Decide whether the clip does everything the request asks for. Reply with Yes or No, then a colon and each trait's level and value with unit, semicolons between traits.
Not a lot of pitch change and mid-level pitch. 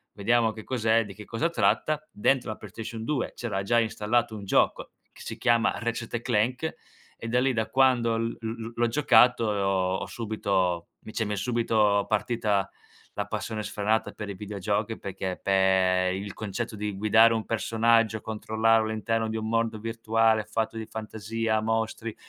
No: narrow, 1.8 semitones; low, 110 Hz